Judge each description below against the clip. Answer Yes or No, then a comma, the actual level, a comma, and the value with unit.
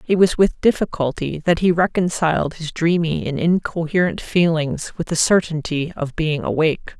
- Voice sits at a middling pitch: Yes, medium, 165 Hz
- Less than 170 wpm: Yes, average, 155 wpm